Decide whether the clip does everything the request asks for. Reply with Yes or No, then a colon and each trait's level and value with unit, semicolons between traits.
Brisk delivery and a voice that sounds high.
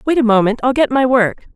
Yes: fast, 270 wpm; high, 245 Hz